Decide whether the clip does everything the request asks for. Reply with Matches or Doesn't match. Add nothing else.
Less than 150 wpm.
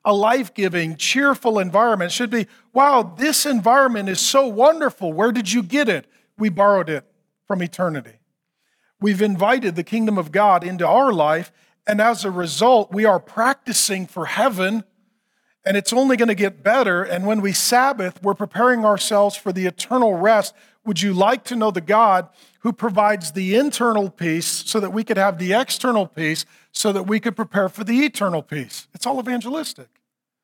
Doesn't match